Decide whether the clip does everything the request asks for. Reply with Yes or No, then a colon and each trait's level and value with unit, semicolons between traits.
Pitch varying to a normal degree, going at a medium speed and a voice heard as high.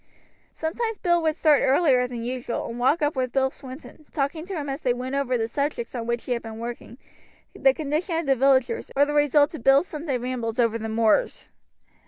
No: average, 3.7 semitones; fast, 215 wpm; very high, 270 Hz